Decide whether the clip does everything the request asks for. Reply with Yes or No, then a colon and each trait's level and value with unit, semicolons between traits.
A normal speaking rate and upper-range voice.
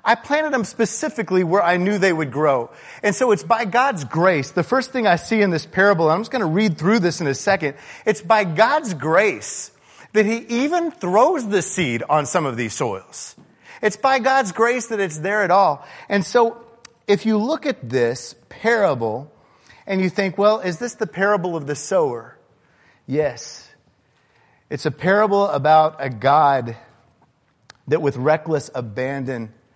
Yes: average, 180 wpm; high, 195 Hz